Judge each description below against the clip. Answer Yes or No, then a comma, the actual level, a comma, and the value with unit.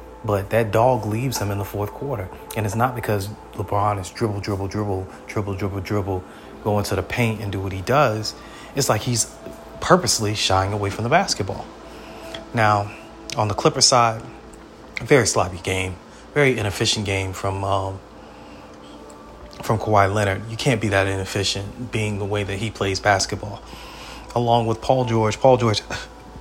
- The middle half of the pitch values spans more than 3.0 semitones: No, average, 2.7 semitones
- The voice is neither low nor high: No, low, 105 Hz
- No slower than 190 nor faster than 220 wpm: No, average, 170 wpm